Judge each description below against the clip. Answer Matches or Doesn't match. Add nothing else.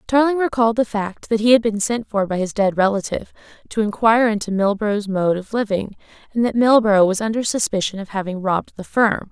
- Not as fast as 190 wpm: Doesn't match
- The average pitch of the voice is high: Matches